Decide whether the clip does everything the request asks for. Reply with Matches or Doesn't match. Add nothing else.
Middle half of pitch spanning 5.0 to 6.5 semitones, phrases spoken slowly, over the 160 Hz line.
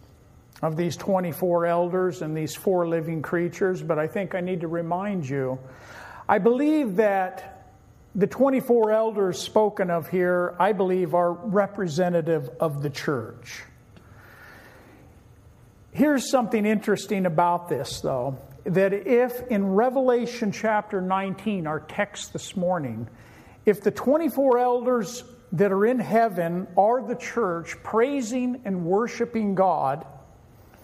Matches